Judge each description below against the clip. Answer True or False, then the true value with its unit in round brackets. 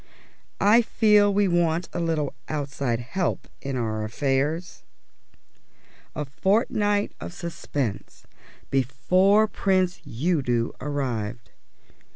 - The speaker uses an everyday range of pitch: False (6.5 semitones)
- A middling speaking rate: False (95 wpm)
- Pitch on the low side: False (155 Hz)